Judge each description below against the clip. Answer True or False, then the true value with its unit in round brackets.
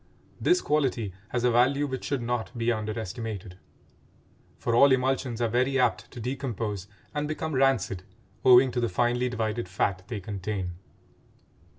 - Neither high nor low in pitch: False (120 Hz)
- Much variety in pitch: False (3.3 semitones)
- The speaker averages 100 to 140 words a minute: False (150 wpm)